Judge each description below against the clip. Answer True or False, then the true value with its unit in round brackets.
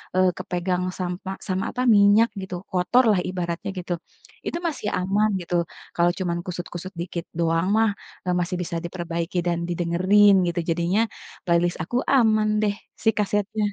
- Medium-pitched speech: True (180 Hz)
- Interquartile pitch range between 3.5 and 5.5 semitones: False (2.8 semitones)